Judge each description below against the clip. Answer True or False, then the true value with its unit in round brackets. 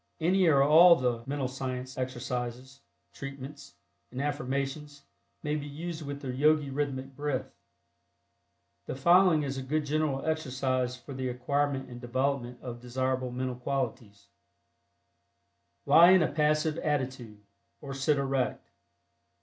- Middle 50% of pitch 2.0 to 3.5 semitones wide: True (2.5 semitones)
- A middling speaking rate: False (130 wpm)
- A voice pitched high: False (135 Hz)